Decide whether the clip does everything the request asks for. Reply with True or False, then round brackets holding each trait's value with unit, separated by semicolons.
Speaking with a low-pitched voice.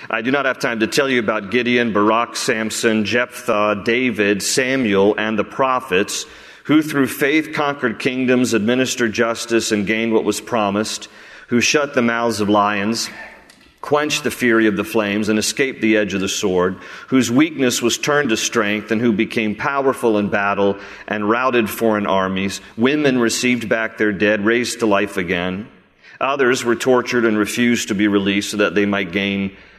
True (110 Hz)